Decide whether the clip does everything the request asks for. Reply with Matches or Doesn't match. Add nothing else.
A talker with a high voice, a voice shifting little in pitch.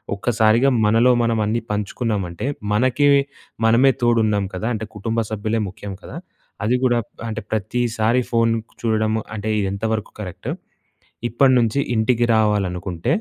Doesn't match